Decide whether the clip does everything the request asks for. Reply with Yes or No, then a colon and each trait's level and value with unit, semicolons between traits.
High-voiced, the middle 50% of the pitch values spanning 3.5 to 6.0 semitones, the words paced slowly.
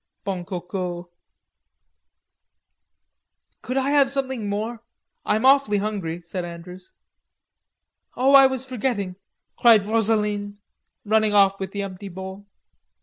Yes: high, 205 Hz; average, 4.1 semitones; slow, 110 wpm